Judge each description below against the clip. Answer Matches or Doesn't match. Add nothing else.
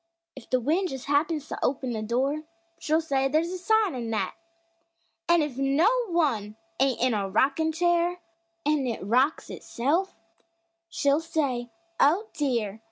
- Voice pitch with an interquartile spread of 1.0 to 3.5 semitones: Doesn't match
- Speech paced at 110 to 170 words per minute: Matches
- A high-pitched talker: Matches